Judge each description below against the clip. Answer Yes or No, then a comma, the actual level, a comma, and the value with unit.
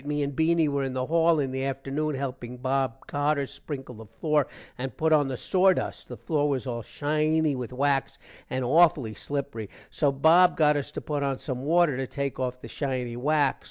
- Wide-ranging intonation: No, average, 2.8 semitones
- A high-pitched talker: No, medium, 140 Hz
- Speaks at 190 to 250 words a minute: Yes, average, 200 wpm